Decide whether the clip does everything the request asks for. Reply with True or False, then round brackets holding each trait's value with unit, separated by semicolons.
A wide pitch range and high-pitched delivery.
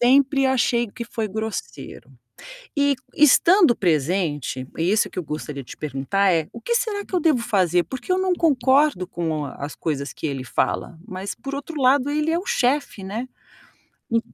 True (8.6 semitones; 235 Hz)